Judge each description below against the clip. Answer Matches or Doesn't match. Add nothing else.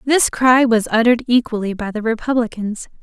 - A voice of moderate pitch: Doesn't match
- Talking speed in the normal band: Matches